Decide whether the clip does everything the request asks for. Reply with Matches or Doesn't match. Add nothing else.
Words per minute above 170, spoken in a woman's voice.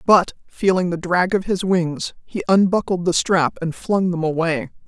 Matches